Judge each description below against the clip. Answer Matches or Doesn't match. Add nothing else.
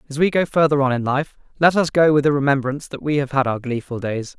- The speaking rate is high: Matches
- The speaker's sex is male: Matches